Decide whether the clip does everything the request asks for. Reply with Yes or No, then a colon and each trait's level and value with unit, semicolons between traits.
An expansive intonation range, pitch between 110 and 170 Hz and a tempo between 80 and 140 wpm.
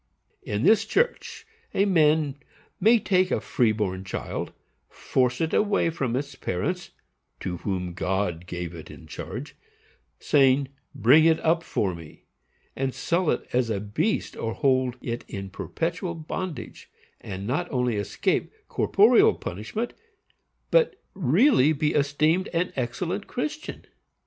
Yes: wide, 9.0 semitones; medium, 140 Hz; slow, 135 wpm